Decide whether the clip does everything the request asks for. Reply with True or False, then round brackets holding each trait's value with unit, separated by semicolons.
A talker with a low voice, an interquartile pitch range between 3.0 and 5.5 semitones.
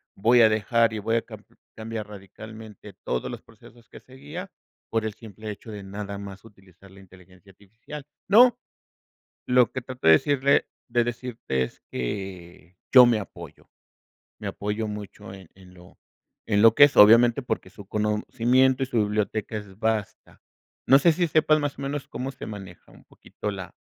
True (110 Hz; 4.0 semitones)